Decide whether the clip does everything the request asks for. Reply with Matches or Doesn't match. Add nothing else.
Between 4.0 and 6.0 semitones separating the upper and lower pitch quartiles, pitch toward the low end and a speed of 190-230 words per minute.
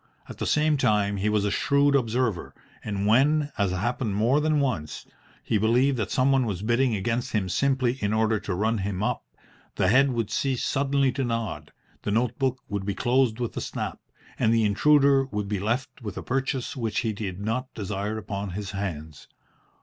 Matches